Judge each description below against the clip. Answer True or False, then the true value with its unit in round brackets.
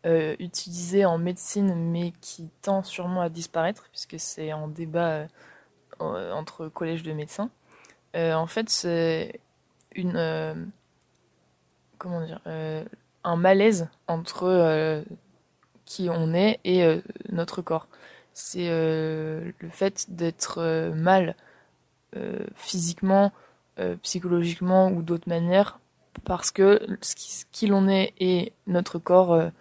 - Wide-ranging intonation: False (2.7 semitones)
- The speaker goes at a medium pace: False (130 wpm)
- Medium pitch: True (175 Hz)